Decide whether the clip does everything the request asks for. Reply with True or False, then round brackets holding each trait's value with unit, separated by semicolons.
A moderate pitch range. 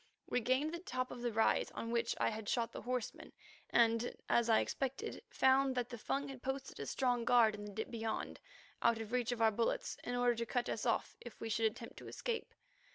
False (2.1 semitones)